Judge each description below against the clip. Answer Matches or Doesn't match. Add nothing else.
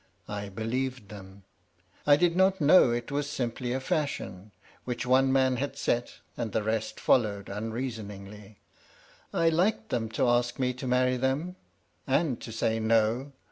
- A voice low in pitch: Matches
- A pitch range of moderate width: Matches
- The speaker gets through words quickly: Doesn't match